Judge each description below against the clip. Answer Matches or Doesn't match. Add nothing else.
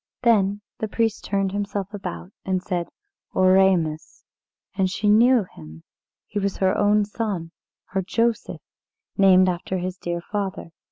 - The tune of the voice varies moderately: Doesn't match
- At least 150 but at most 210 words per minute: Doesn't match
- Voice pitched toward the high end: Matches